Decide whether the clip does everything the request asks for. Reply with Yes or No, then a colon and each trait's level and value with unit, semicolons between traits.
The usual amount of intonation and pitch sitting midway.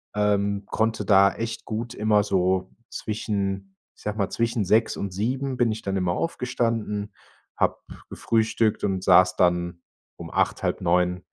No: average, 3.1 semitones; low, 105 Hz